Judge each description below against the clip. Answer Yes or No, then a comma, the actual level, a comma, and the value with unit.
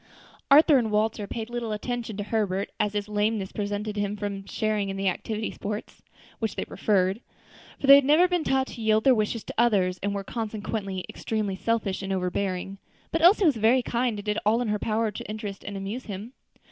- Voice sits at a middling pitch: No, high, 215 Hz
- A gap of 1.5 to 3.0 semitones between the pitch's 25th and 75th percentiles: Yes, narrow, 2.6 semitones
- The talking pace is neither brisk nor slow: No, fast, 210 wpm